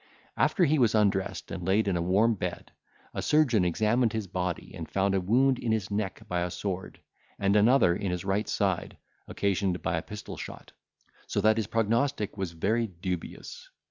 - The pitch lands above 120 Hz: No, low, 100 Hz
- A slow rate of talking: No, average, 185 wpm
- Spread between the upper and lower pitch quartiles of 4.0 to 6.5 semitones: No, average, 3.4 semitones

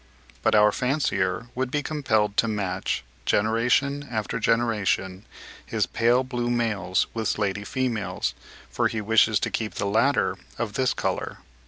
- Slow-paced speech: No, average, 145 wpm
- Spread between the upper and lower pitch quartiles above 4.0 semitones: No, average, 3.2 semitones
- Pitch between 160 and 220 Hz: No, low, 110 Hz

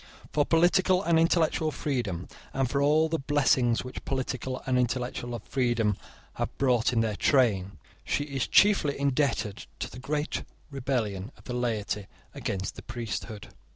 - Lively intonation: No, average, 4.1 semitones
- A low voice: Yes, low, 130 Hz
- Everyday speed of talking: Yes, average, 150 wpm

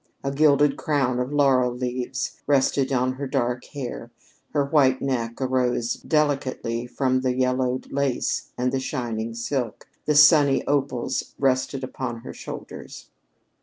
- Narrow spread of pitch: Yes, narrow, 2.0 semitones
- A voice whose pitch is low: Yes, low, 130 Hz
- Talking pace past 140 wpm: No, slow, 135 wpm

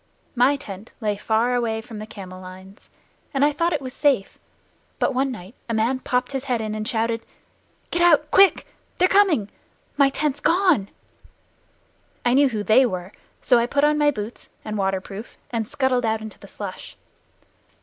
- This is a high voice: Yes, high, 240 Hz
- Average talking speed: Yes, average, 180 wpm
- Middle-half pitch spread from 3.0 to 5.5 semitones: Yes, average, 4.8 semitones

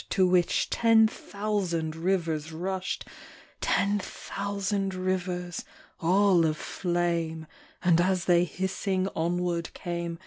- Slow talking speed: Yes, slow, 115 wpm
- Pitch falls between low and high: Yes, medium, 180 Hz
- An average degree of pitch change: No, narrow, 2.2 semitones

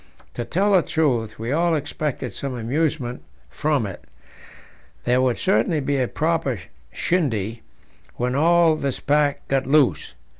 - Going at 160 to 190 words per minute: No, average, 140 wpm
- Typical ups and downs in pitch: Yes, average, 4.3 semitones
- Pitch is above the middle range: No, medium, 140 Hz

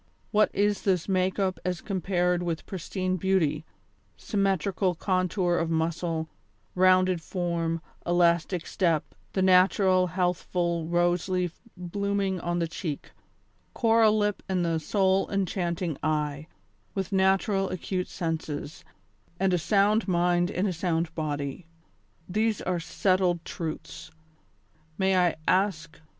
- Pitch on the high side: No, medium, 180 Hz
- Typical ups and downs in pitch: No, narrow, 2.2 semitones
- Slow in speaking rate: Yes, slow, 120 wpm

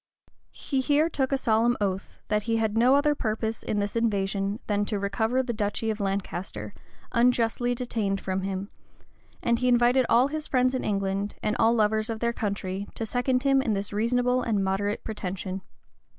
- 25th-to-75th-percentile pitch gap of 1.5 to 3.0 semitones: No, average, 3.6 semitones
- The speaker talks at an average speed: Yes, average, 180 wpm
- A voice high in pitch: Yes, high, 220 Hz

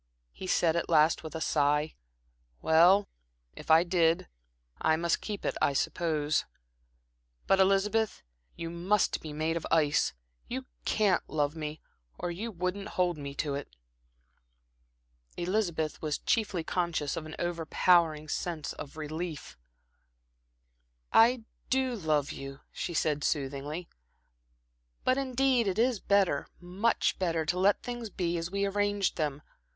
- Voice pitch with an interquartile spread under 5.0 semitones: Yes, average, 4.2 semitones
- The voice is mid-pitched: Yes, medium, 170 Hz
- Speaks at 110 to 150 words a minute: Yes, slow, 135 wpm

